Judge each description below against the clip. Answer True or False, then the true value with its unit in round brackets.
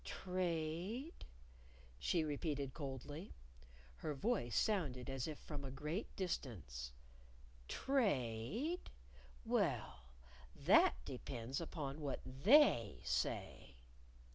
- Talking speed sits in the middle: False (90 wpm)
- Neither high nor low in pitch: True (150 Hz)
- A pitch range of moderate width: False (6.0 semitones)